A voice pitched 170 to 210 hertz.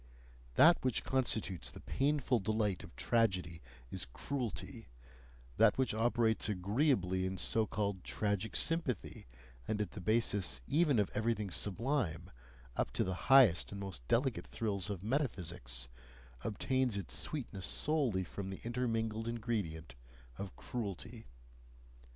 No: low, 110 Hz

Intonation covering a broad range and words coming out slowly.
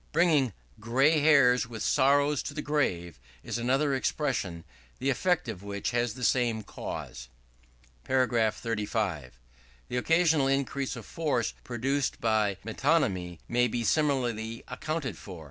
No: average, 4.4 semitones; slow, 130 wpm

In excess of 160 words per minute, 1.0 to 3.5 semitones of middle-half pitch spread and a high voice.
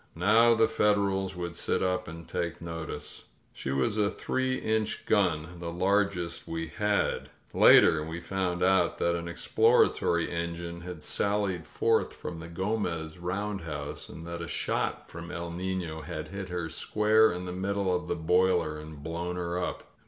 No: average, 170 wpm; average, 2.8 semitones; very low, 90 Hz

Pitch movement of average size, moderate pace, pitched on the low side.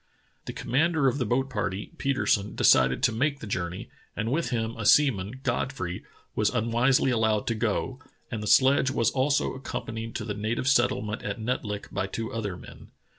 Yes: average, 3.8 semitones; average, 180 wpm; low, 115 Hz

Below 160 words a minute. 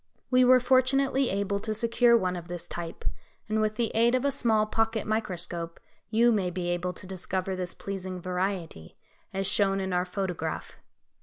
No: average, 175 wpm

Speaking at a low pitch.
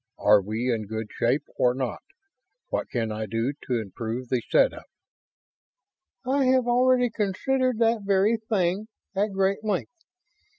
No: high, 190 Hz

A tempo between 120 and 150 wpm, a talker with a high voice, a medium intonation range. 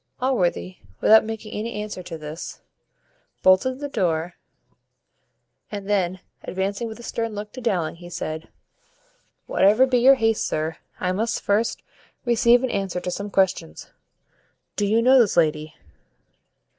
Yes: average, 145 wpm; high, 205 Hz; average, 4.7 semitones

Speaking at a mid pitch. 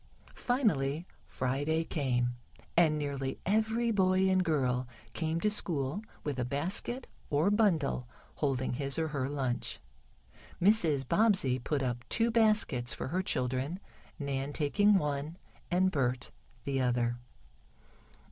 Yes: medium, 145 Hz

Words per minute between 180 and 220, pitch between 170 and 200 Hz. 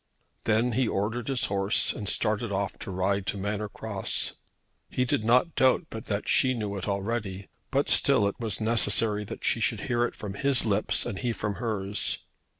No: average, 190 wpm; low, 105 Hz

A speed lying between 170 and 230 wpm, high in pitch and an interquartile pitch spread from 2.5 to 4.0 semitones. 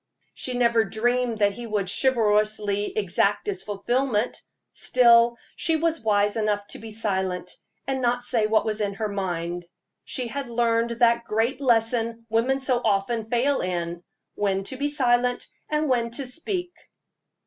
No: average, 155 wpm; high, 230 Hz; average, 3.1 semitones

